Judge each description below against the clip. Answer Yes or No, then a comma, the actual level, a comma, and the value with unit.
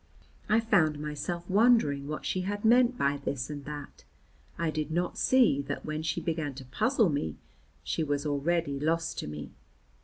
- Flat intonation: No, average, 4.3 semitones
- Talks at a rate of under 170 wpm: No, average, 175 wpm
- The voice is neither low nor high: Yes, medium, 155 Hz